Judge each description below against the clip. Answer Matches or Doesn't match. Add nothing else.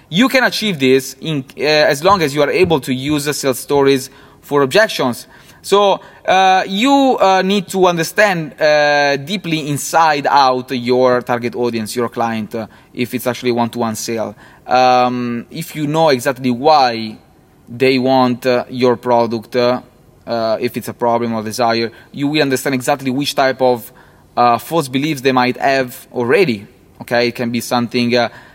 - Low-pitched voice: Matches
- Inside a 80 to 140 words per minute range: Doesn't match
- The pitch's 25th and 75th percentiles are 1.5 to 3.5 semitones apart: Doesn't match